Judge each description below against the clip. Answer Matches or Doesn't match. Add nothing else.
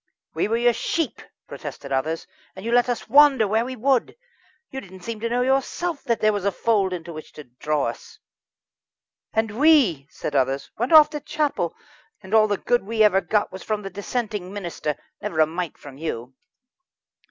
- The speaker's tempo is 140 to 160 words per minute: Doesn't match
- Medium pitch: Doesn't match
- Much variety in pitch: Matches